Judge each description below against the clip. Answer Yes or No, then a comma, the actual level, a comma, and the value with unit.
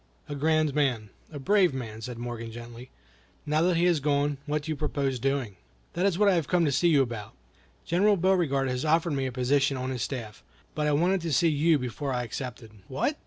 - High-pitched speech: No, medium, 140 Hz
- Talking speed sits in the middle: No, fast, 220 wpm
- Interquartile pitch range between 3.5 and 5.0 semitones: Yes, average, 4.5 semitones